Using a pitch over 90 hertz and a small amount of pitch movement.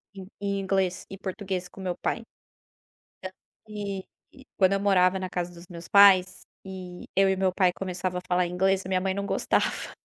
Yes: high, 190 Hz; narrow, 1.3 semitones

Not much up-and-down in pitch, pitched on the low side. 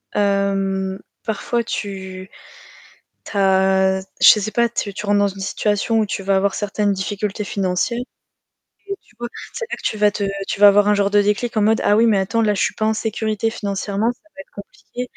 No: narrow, 1.9 semitones; high, 205 Hz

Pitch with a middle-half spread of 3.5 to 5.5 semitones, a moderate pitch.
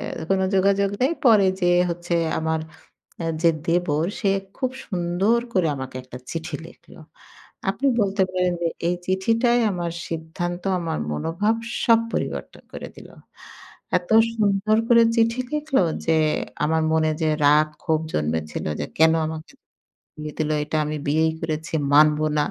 Yes: average, 4.1 semitones; medium, 170 Hz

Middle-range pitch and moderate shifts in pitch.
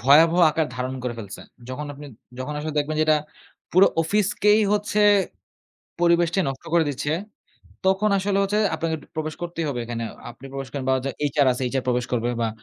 Yes: medium, 155 Hz; average, 4.9 semitones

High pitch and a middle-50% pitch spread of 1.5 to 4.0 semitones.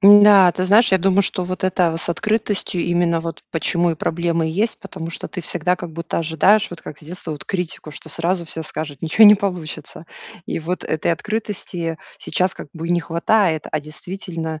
No: medium, 175 Hz; average, 2.8 semitones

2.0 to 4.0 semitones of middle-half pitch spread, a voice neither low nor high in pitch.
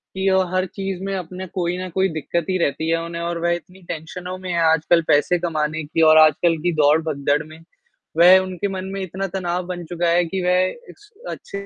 Yes: narrow, 2.5 semitones; medium, 175 Hz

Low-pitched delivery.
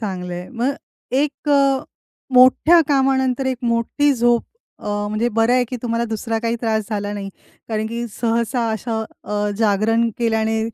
No: high, 230 Hz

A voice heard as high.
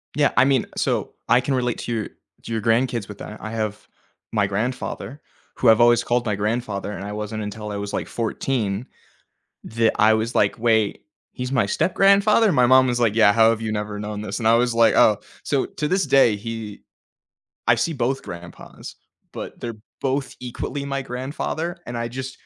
No: low, 115 Hz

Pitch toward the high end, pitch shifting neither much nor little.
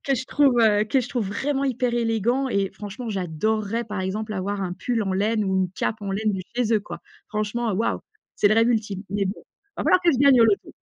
Yes: high, 215 Hz; average, 3.3 semitones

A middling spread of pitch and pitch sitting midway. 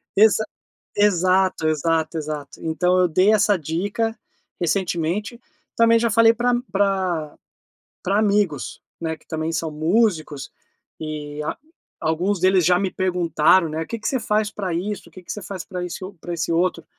Yes: average, 4.1 semitones; medium, 180 Hz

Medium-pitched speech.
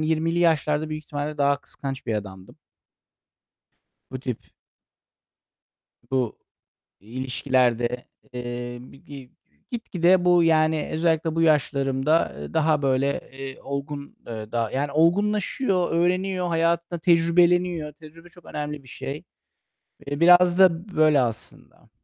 Yes: medium, 150 Hz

